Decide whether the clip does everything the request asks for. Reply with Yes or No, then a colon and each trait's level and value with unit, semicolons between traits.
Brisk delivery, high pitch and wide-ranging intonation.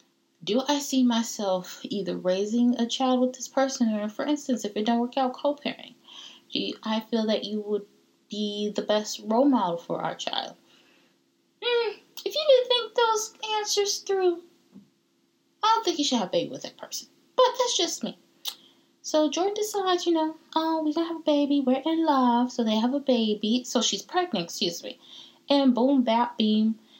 No: average, 185 wpm; very high, 260 Hz; wide, 6.8 semitones